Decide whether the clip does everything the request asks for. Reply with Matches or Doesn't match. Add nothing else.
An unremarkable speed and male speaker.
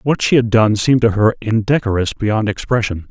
Matches